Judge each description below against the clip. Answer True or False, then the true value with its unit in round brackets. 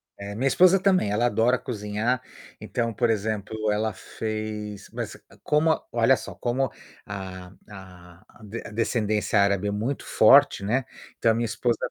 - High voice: False (110 Hz)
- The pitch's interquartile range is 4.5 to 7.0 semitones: False (2.8 semitones)